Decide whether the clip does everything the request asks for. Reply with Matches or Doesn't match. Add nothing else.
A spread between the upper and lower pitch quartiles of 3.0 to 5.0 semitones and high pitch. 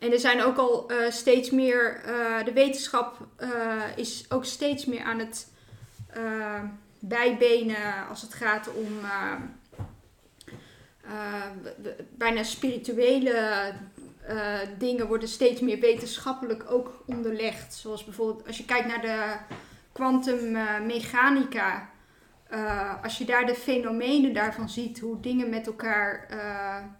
Doesn't match